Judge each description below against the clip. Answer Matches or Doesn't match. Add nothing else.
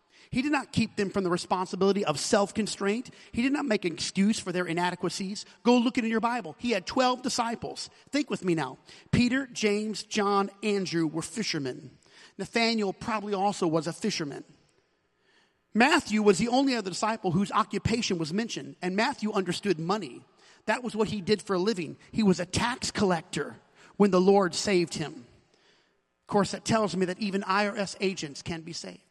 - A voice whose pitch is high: Matches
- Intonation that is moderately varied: Matches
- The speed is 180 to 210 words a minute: Matches